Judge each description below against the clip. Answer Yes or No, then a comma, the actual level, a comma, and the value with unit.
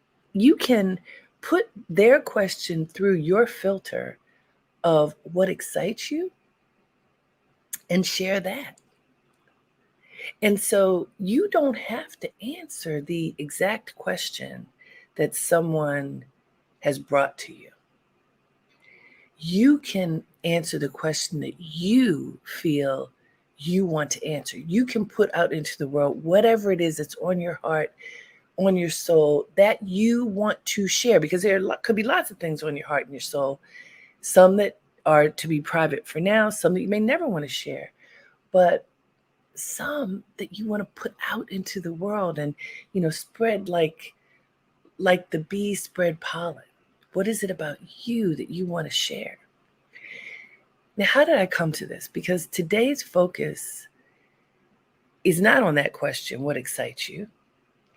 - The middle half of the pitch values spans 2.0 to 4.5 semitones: No, average, 5.1 semitones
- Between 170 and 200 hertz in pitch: Yes, medium, 185 Hz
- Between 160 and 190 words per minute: No, average, 150 wpm